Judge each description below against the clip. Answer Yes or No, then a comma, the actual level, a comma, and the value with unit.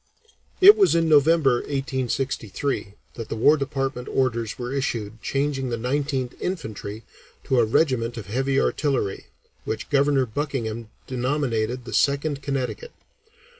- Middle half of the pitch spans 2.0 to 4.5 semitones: Yes, average, 3.4 semitones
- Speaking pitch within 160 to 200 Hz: No, low, 130 Hz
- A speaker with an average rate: No, slow, 130 wpm